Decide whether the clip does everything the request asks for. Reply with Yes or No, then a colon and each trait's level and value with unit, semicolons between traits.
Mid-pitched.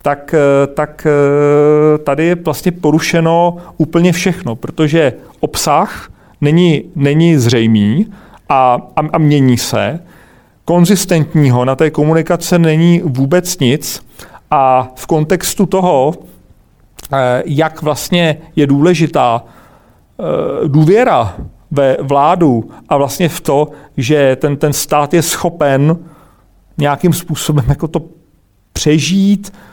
Yes: medium, 155 Hz